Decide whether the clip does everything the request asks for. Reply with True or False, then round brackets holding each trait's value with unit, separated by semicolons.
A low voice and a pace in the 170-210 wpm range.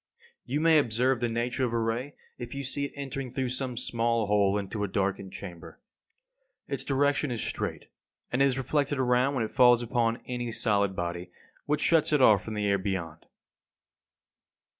True (120 Hz; 180 wpm)